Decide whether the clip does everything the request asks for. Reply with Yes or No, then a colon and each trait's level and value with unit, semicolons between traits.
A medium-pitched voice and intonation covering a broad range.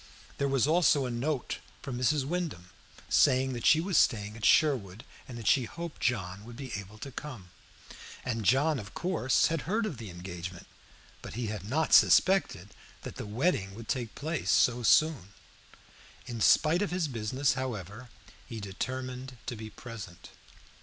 No: low, 125 Hz; wide, 5.8 semitones